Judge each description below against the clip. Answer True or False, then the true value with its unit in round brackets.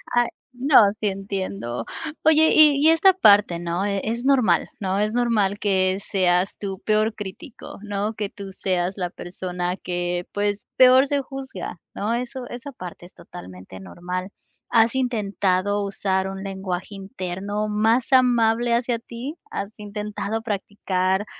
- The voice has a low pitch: False (205 Hz)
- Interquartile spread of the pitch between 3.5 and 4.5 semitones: True (4.0 semitones)